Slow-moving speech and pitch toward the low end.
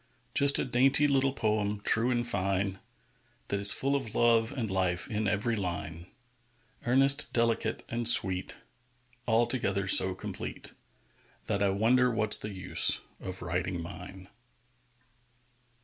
Yes: slow, 130 wpm; low, 105 Hz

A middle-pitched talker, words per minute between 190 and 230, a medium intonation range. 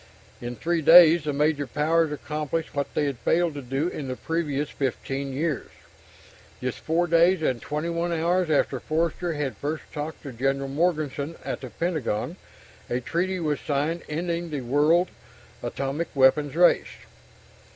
No: medium, 150 Hz; average, 150 wpm; average, 3.3 semitones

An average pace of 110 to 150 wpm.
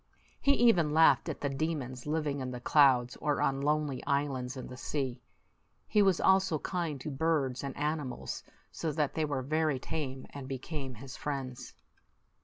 No: average, 170 wpm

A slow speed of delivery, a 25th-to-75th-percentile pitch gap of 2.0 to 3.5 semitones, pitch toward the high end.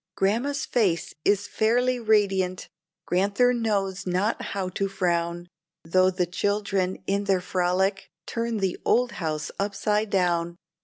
Yes: slow, 125 wpm; average, 2.7 semitones; high, 195 Hz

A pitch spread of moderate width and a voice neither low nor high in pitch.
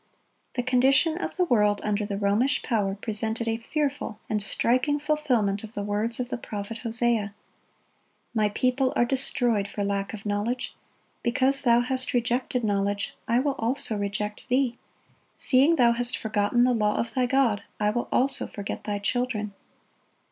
No: average, 3.5 semitones; high, 235 Hz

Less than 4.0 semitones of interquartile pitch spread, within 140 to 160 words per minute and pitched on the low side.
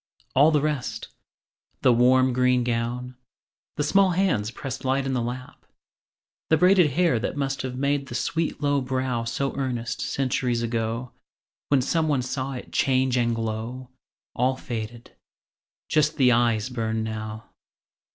Yes: average, 2.7 semitones; average, 150 wpm; low, 130 Hz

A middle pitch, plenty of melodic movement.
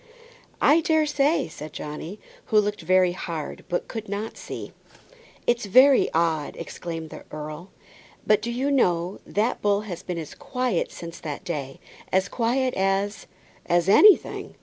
No: high, 195 Hz; wide, 6.0 semitones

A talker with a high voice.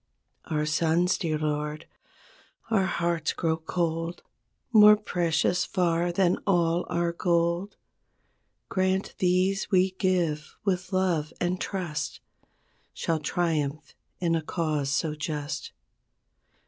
No: medium, 170 Hz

